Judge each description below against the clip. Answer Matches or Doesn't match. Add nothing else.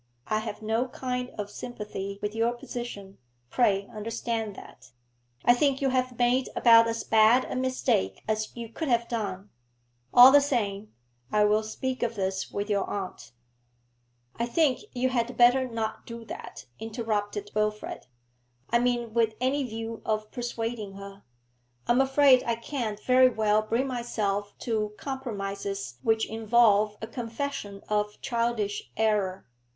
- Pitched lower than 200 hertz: Doesn't match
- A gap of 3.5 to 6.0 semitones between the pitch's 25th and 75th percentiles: Doesn't match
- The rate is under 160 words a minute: Matches